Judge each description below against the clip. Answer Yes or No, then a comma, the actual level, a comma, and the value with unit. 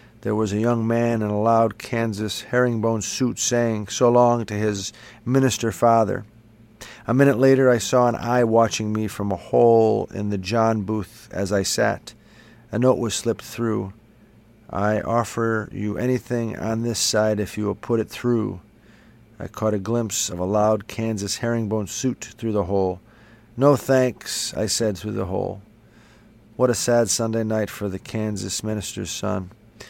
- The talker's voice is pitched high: No, low, 110 Hz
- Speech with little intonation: Yes, narrow, 1.9 semitones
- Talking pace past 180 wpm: No, average, 170 wpm